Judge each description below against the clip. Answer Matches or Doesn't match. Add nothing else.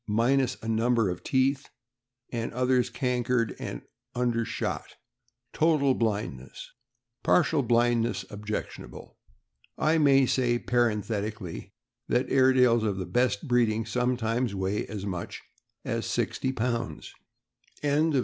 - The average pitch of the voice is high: Doesn't match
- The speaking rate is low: Matches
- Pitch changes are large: Doesn't match